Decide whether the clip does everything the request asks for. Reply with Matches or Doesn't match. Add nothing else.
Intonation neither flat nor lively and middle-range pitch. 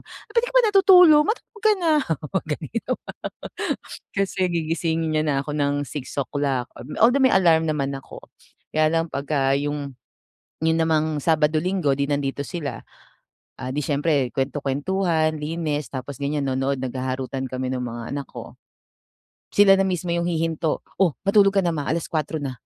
Matches